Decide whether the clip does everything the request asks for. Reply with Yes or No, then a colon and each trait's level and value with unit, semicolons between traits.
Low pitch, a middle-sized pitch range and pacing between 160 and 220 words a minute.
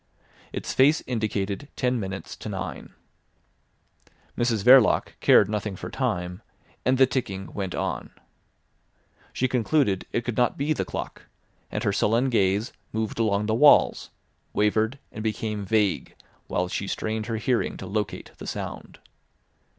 No: low, 110 Hz; average, 3.7 semitones; average, 145 wpm